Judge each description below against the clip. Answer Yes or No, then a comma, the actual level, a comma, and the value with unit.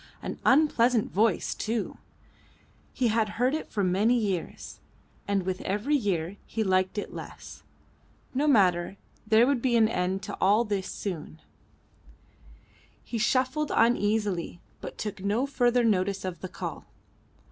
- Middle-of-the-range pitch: No, high, 210 Hz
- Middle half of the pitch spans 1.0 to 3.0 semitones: No, average, 4.1 semitones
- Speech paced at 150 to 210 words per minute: No, average, 140 wpm